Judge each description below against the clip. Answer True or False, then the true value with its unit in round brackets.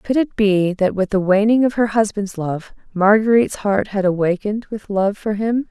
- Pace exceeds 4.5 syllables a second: True (4.9 syllables/s)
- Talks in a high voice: True (205 Hz)